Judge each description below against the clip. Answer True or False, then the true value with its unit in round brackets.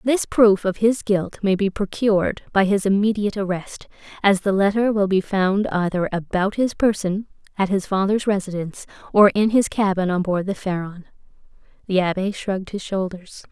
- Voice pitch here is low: False (195 Hz)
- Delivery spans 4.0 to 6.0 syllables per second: True (5.1 syllables/s)